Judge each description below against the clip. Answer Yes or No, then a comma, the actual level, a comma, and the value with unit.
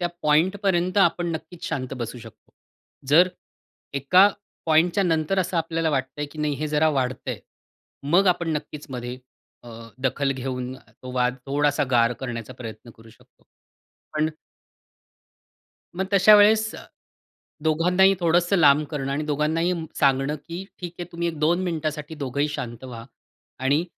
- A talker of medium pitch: Yes, medium, 150 Hz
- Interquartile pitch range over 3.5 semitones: Yes, average, 4.6 semitones